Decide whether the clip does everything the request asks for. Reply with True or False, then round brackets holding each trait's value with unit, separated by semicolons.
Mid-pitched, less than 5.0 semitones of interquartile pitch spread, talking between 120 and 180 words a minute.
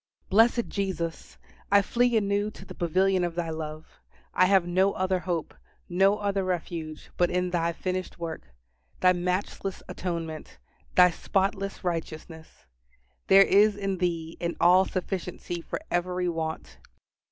True (180 Hz; 2.4 semitones; 140 wpm)